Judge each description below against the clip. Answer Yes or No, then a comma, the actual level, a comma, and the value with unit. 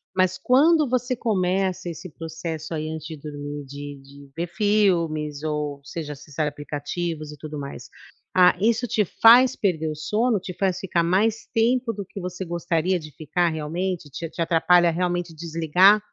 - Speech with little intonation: No, average, 3.9 semitones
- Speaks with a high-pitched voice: No, medium, 170 Hz